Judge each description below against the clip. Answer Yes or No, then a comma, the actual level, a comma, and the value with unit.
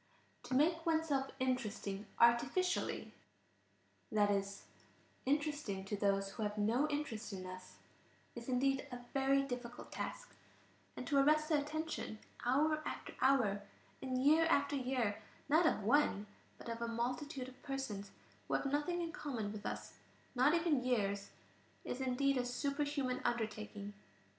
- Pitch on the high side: Yes, very high, 255 Hz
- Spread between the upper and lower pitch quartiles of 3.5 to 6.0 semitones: Yes, average, 5.1 semitones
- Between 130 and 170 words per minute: Yes, average, 145 wpm